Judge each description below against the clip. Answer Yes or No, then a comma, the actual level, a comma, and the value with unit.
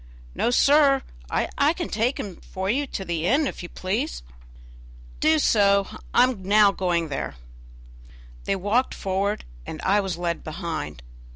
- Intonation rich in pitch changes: Yes, wide, 6.0 semitones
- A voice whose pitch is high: Yes, high, 200 Hz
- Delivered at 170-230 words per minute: No, average, 155 wpm